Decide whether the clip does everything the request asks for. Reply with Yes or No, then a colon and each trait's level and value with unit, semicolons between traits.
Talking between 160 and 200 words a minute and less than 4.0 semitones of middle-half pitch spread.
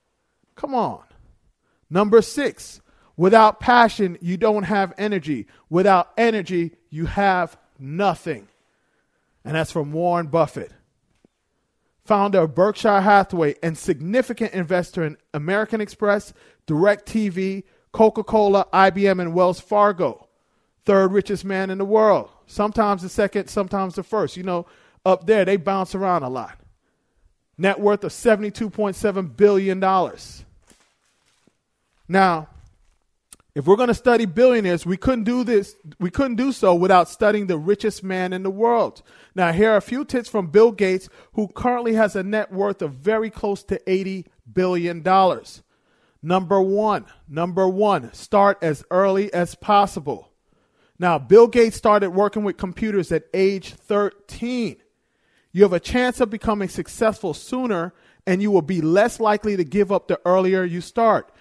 No: average, 145 wpm; average, 2.8 semitones